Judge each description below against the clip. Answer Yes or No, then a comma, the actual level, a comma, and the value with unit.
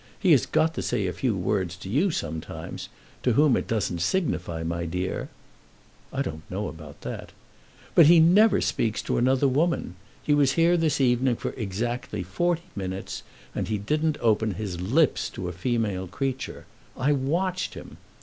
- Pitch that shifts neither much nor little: No, wide, 8.4 semitones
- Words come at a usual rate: Yes, average, 175 wpm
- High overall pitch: No, low, 120 Hz